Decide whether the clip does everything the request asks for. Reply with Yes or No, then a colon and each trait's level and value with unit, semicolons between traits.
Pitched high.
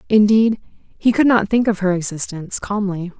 Yes: high, 205 Hz